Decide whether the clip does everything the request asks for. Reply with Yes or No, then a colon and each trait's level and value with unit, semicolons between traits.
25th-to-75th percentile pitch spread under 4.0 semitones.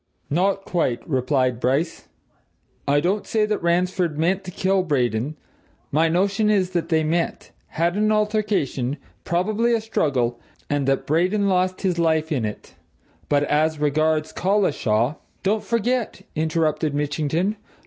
No: average, 4.9 semitones